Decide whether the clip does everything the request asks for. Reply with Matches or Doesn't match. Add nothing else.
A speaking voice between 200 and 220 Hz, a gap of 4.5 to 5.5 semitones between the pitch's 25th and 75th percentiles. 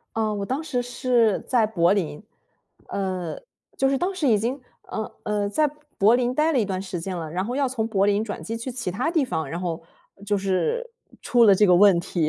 Matches